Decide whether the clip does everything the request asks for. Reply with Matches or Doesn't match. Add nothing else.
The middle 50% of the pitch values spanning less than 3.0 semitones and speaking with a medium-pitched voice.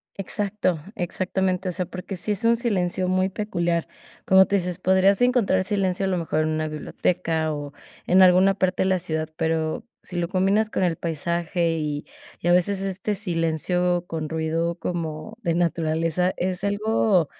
Matches